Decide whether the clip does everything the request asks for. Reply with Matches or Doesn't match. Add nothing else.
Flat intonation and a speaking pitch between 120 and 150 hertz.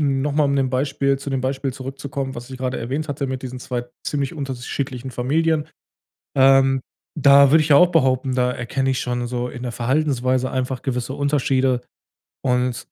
Matches